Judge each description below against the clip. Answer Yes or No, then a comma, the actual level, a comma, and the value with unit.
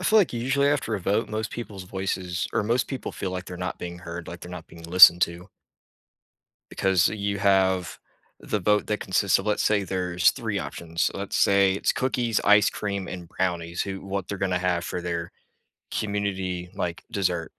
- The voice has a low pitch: Yes, very low, 95 Hz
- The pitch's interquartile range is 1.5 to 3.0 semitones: Yes, narrow, 2.6 semitones